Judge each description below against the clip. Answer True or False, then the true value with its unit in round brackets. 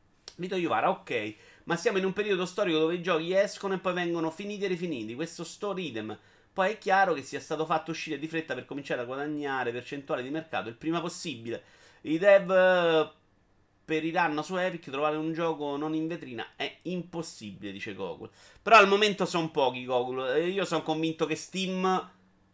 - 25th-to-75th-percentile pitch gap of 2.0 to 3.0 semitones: False (4.5 semitones)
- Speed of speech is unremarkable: False (185 wpm)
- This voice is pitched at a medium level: True (160 Hz)